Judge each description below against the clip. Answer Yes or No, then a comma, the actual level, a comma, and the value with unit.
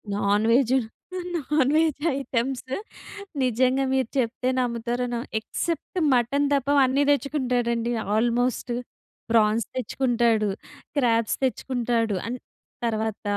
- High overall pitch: Yes, high, 245 Hz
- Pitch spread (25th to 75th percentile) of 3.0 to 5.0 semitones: No, narrow, 2.5 semitones